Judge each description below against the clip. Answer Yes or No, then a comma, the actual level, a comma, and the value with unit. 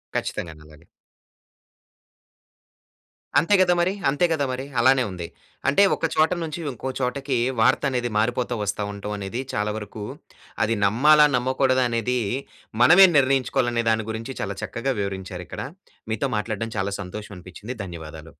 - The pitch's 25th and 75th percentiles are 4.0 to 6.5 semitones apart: Yes, average, 4.8 semitones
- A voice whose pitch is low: Yes, low, 120 Hz